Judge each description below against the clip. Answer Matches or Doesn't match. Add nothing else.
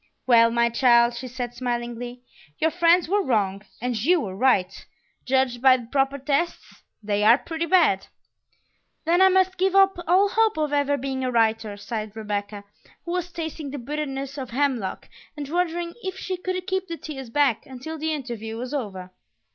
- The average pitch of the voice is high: Matches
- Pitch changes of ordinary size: Doesn't match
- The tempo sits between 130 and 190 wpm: Matches